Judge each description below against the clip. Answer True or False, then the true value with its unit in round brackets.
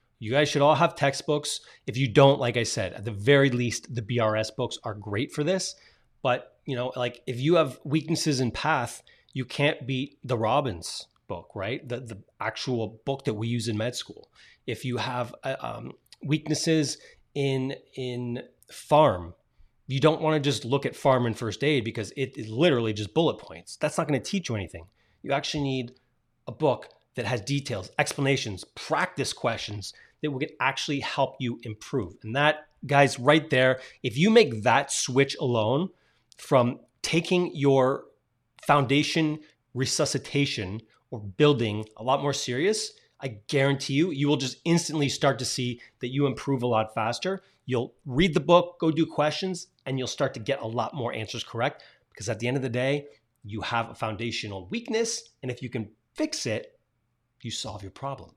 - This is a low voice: True (130 Hz)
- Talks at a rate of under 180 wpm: False (185 wpm)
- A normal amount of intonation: True (4.0 semitones)